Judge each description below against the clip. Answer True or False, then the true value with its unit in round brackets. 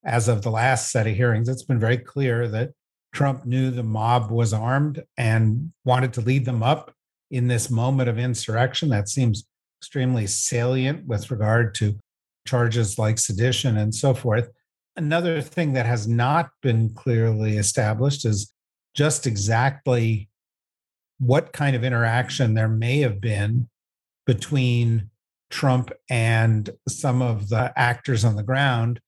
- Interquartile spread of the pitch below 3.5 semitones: True (2.7 semitones)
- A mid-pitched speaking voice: False (120 Hz)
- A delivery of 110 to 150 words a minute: True (145 wpm)